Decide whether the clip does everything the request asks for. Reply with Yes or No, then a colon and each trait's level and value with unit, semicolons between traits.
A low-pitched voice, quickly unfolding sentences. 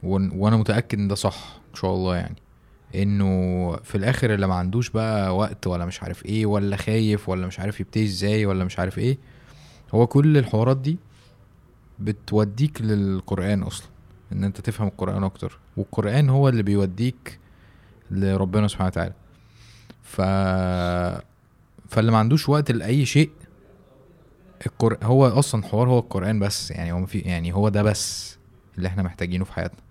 Yes: low, 100 Hz; fast, 155 wpm